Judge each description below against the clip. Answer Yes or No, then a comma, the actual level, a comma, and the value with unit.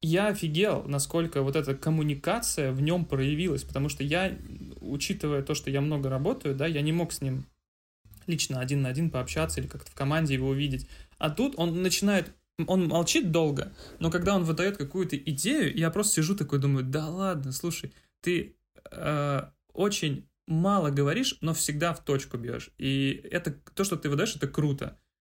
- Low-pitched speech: No, medium, 155 Hz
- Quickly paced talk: Yes, fast, 175 wpm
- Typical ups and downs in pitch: Yes, average, 3.9 semitones